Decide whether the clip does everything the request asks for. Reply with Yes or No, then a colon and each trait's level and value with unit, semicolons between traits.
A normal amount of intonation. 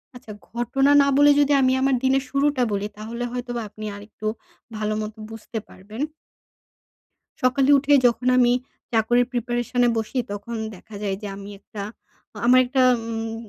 Yes: average, 3.3 semitones